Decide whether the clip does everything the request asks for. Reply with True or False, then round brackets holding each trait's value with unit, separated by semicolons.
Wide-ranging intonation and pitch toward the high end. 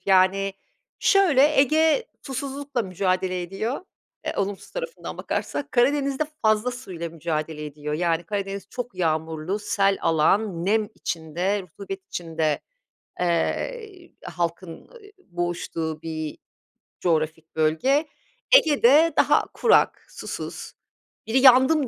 True (8.1 semitones; 195 Hz)